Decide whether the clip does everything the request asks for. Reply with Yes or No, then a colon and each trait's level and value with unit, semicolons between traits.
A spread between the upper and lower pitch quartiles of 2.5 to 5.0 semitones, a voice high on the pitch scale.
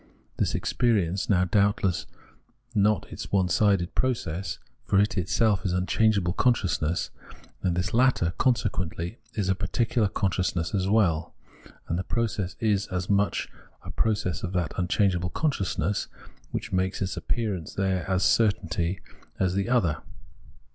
No: average, 2.9 semitones; very low, 95 Hz